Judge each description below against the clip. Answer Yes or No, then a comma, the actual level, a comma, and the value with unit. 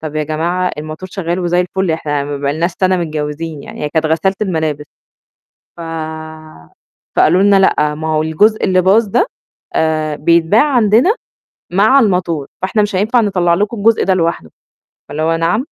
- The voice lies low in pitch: No, medium, 175 Hz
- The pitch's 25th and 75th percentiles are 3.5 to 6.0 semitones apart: Yes, average, 3.9 semitones